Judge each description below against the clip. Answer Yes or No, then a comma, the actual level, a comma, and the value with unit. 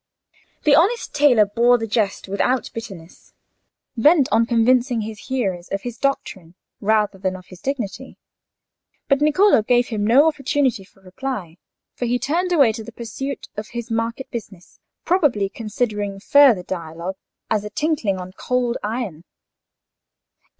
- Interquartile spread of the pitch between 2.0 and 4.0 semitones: No, average, 4.9 semitones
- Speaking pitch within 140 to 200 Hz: No, high, 230 Hz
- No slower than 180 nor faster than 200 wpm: No, average, 145 wpm